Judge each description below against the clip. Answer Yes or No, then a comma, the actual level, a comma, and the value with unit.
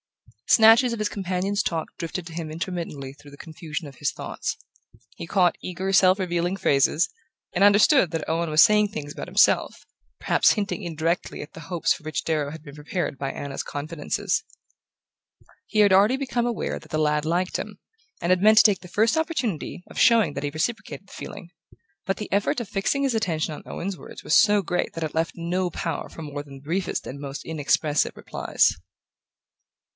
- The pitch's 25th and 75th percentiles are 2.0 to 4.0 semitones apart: No, average, 4.7 semitones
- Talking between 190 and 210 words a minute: Yes, average, 195 wpm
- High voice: No, medium, 175 Hz